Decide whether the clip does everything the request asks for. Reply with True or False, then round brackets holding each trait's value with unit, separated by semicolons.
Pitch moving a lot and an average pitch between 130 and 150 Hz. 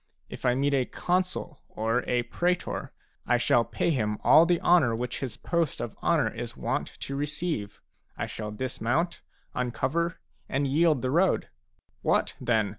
True (5.8 semitones; 135 Hz)